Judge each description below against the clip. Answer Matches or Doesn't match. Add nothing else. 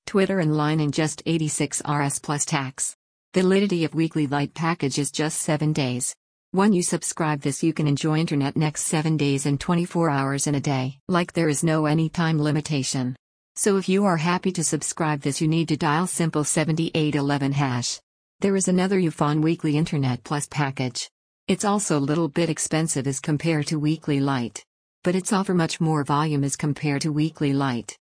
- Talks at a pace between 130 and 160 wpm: Doesn't match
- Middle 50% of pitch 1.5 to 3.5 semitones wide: Matches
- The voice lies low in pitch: Doesn't match